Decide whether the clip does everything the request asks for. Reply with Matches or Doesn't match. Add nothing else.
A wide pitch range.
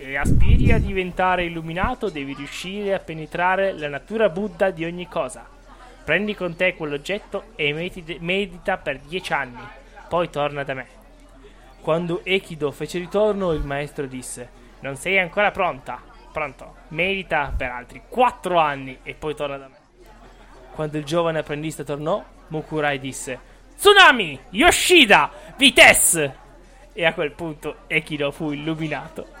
Doesn't match